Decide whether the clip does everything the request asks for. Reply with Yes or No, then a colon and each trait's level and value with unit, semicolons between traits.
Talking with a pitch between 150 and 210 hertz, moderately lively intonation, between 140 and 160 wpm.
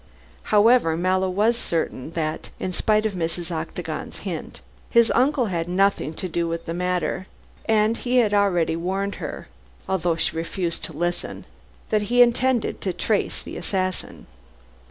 Yes: medium, 185 Hz; average, 4.2 semitones; average, 155 wpm